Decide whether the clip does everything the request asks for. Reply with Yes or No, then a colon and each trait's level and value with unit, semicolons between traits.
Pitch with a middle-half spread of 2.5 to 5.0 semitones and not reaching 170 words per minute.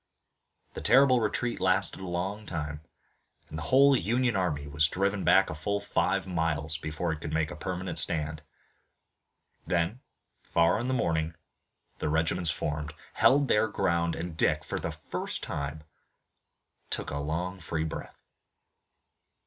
Yes: average, 4.1 semitones; average, 150 wpm